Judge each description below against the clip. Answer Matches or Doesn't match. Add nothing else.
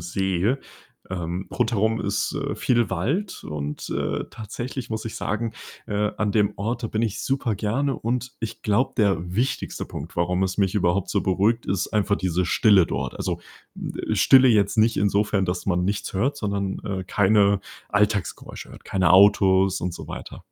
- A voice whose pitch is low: Matches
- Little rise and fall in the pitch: Doesn't match